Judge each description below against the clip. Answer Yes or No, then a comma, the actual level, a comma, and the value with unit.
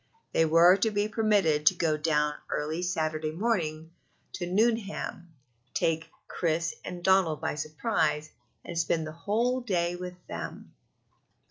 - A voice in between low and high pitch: Yes, medium, 170 Hz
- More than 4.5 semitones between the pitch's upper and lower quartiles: No, average, 4.0 semitones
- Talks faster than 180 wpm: No, slow, 135 wpm